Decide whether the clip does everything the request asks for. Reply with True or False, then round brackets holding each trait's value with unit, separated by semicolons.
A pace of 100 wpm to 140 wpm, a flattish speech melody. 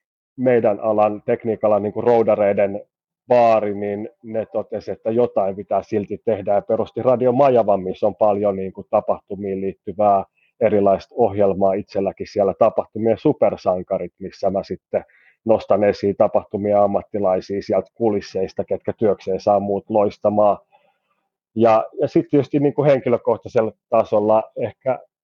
True (125 wpm; 2.3 semitones)